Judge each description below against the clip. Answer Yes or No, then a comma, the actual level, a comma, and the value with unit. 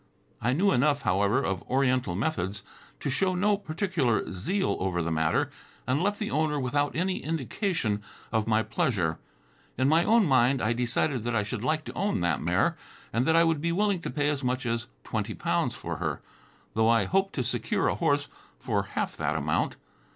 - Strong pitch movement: Yes, wide, 7.2 semitones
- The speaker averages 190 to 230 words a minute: Yes, average, 195 wpm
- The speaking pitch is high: No, low, 130 Hz